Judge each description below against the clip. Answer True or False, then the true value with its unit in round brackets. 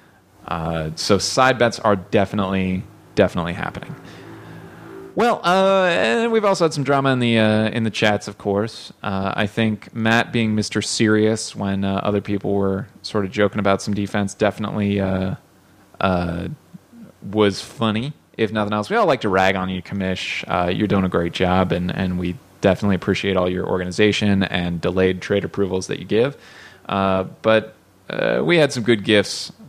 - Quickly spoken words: False (175 wpm)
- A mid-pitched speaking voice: False (100 Hz)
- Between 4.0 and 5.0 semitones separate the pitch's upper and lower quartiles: False (2.6 semitones)